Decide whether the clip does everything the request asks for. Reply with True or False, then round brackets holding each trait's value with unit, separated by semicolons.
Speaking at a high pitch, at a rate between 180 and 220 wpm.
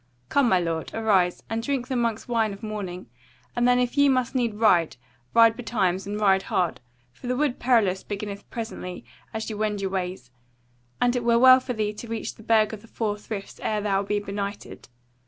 True (215 Hz; 205 wpm)